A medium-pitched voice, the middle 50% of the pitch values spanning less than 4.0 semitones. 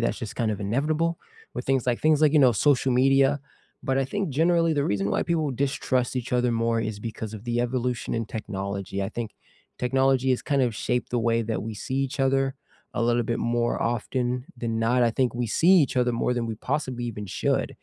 No: low, 125 Hz; average, 2.8 semitones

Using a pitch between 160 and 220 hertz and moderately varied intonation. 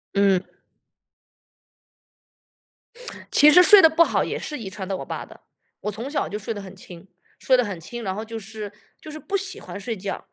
No: high, 215 Hz; wide, 6.9 semitones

